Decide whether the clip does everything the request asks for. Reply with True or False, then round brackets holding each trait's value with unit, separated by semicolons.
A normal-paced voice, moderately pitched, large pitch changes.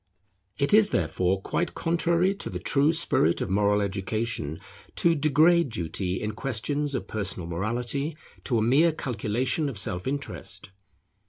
False (145 wpm; 120 Hz; 7.7 semitones)